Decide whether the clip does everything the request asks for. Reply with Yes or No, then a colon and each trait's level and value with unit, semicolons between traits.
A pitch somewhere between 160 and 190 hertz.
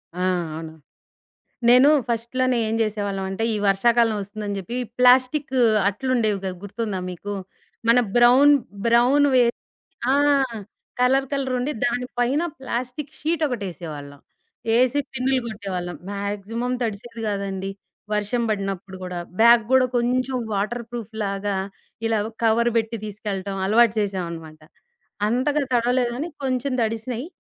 No: high, 230 Hz